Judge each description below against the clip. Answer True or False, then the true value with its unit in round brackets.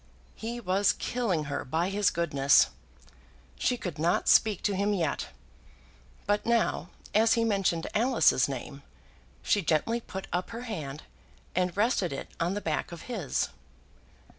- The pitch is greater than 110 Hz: True (190 Hz)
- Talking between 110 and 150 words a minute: True (145 wpm)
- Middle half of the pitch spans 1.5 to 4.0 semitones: False (5.4 semitones)